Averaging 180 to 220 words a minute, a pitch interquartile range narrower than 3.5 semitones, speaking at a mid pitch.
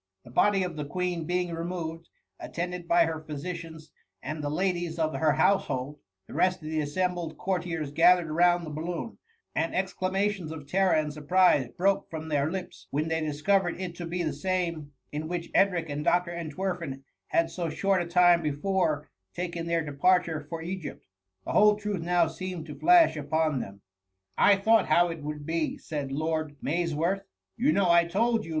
Yes: average, 185 wpm; average, 2.7 semitones; medium, 170 Hz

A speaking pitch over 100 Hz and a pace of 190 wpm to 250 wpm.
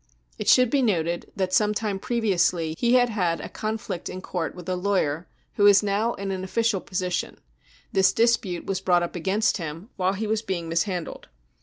Yes: high, 190 Hz; average, 195 wpm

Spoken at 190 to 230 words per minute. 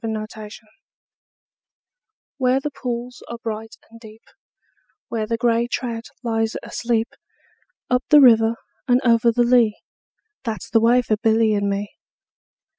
No: average, 145 wpm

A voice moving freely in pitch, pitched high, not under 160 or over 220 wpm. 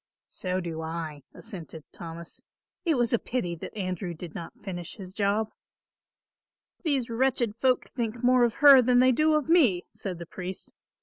Yes: wide, 6.4 semitones; high, 210 Hz; average, 170 wpm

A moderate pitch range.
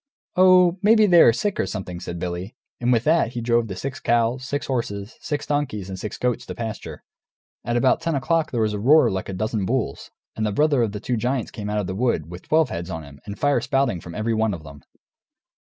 No: wide, 5.8 semitones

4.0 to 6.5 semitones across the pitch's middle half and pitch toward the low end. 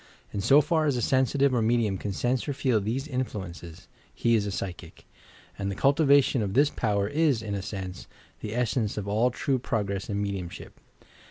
Yes: average, 4.8 semitones; low, 110 Hz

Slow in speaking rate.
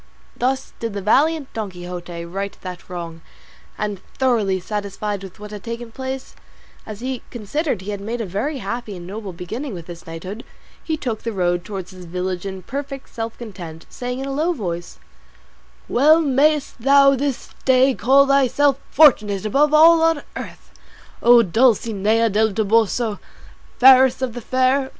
No: average, 165 wpm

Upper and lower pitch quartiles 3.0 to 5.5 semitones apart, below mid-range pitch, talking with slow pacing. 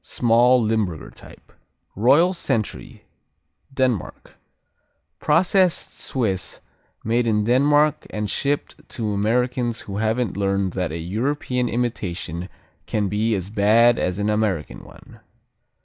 Yes: average, 3.8 semitones; low, 110 Hz; slow, 115 wpm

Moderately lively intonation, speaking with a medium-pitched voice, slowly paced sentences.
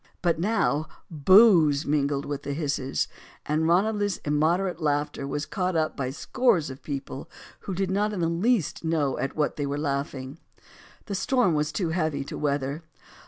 No: average, 4.3 semitones; medium, 155 Hz; average, 165 wpm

